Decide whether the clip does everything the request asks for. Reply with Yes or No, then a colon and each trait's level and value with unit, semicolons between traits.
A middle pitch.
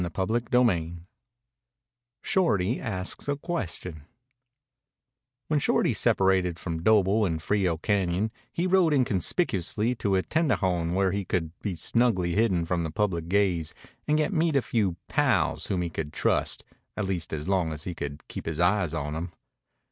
No: very low, 95 Hz